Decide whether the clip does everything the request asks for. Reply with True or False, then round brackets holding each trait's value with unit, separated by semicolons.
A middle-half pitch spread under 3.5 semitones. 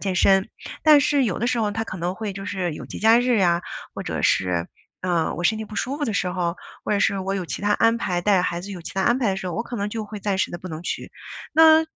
False (4.0 semitones)